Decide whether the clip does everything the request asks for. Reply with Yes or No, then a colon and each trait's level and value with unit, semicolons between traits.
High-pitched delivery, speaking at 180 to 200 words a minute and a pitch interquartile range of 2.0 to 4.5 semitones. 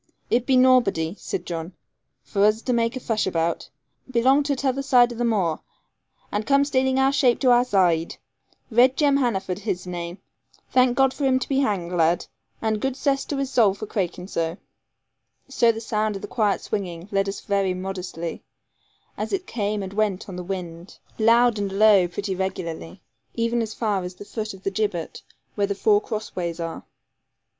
No: high, 210 Hz; average, 190 wpm; average, 4.9 semitones